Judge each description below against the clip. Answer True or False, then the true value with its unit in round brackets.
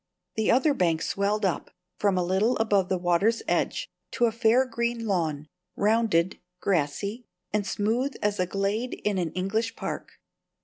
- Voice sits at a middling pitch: False (205 Hz)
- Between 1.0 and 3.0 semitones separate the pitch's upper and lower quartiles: False (3.8 semitones)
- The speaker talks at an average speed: True (160 wpm)